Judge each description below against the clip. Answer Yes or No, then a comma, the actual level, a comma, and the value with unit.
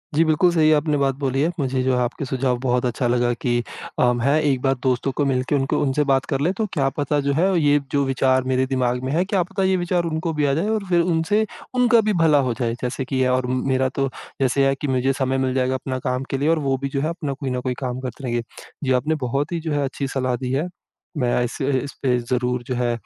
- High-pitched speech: No, low, 135 Hz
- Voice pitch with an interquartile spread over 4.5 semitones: No, average, 3.0 semitones